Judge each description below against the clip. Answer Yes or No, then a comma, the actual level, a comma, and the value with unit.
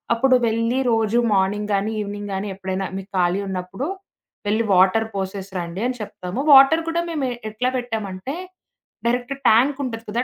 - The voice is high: Yes, high, 215 Hz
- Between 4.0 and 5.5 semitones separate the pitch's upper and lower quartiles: Yes, average, 4.4 semitones